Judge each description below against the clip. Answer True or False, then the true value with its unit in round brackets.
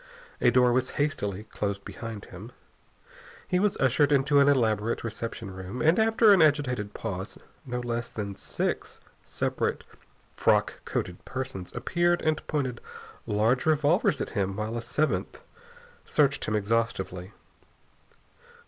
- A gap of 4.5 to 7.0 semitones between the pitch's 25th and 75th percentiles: True (5.6 semitones)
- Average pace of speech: False (130 wpm)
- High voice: False (120 Hz)